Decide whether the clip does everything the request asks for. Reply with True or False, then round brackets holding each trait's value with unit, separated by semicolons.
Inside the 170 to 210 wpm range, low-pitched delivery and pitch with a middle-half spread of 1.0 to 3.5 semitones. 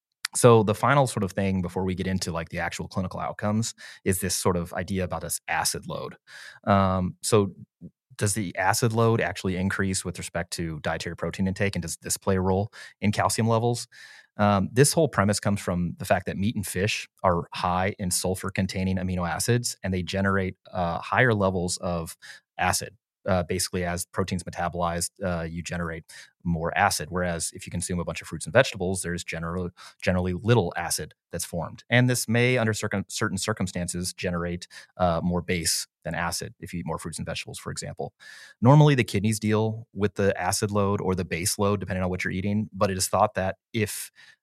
True (195 wpm; 95 Hz; 2.8 semitones)